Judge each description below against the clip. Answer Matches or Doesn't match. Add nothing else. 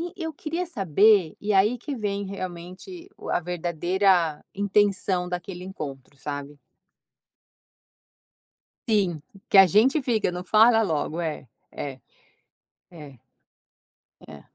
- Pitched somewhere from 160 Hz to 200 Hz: Matches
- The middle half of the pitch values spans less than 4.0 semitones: Doesn't match